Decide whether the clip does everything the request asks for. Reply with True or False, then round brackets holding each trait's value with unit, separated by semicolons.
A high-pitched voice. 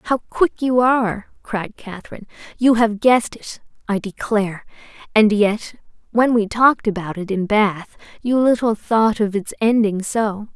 True (220 Hz)